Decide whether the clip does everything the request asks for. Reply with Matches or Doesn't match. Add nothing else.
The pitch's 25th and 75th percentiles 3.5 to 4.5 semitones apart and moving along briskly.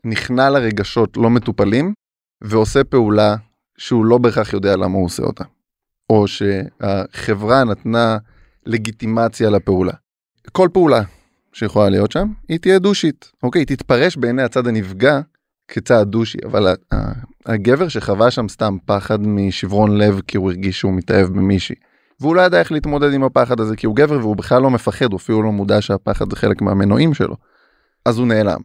Matches